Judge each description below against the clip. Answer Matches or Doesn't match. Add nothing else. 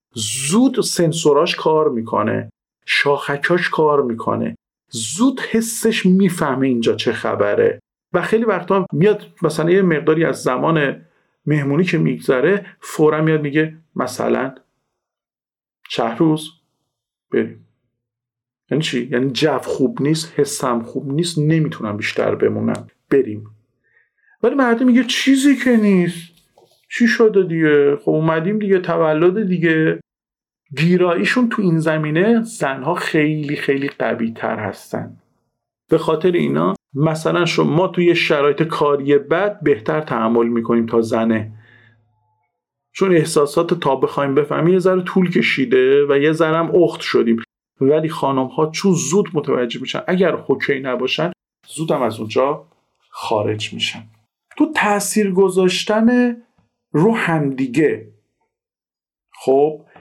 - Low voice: Doesn't match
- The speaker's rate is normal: Matches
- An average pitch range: Doesn't match